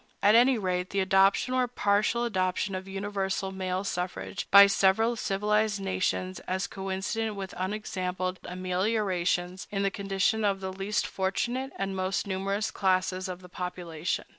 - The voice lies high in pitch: Yes, high, 195 Hz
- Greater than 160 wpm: No, average, 145 wpm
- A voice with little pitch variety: Yes, narrow, 1.8 semitones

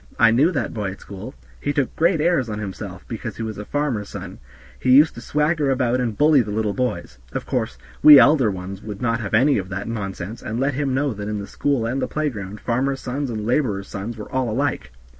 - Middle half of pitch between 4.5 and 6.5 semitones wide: Yes, average, 5.0 semitones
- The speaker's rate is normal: No, fast, 235 wpm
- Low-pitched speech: Yes, low, 115 Hz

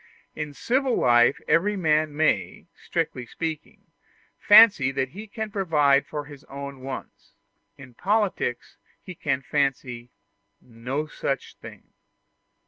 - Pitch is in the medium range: Yes, medium, 150 Hz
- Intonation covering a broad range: Yes, wide, 5.8 semitones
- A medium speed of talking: No, slow, 120 wpm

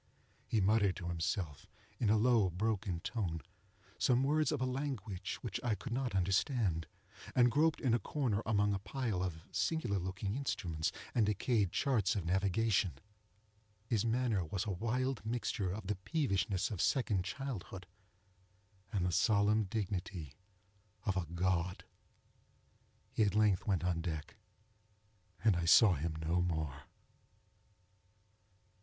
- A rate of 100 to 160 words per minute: Yes, average, 140 wpm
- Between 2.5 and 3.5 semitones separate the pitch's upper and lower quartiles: No, average, 4.5 semitones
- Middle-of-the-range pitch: No, low, 100 Hz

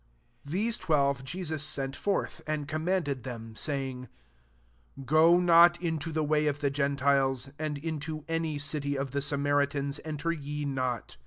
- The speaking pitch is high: No, medium, 145 Hz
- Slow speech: No, average, 155 wpm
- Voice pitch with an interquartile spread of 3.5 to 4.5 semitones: No, narrow, 2.4 semitones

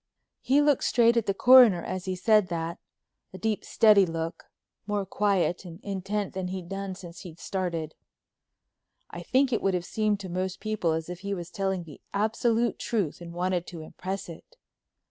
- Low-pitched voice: No, high, 190 Hz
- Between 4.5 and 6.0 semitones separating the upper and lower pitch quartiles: No, average, 3.3 semitones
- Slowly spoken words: No, average, 185 wpm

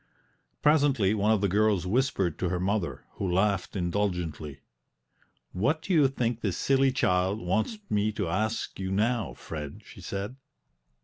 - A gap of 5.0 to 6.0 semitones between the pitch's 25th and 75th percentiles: No, average, 4.1 semitones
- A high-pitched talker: No, low, 100 Hz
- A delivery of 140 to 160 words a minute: Yes, average, 150 wpm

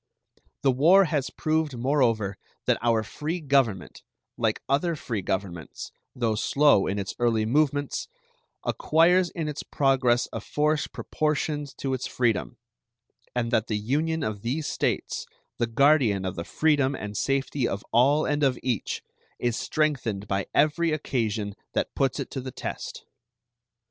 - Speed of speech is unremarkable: Yes, average, 150 wpm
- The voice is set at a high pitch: No, low, 130 Hz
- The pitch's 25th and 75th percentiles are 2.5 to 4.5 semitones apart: No, average, 5.1 semitones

